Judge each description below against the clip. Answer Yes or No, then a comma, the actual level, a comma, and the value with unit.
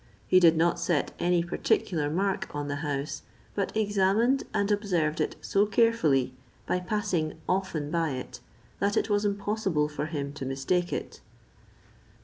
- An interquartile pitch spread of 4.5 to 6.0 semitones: Yes, average, 5.1 semitones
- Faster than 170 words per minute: No, average, 150 wpm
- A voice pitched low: No, medium, 175 Hz